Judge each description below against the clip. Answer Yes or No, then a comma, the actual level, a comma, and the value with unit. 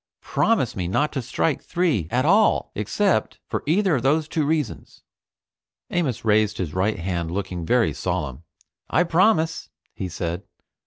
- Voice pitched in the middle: No, low, 130 Hz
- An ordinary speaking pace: Yes, average, 150 wpm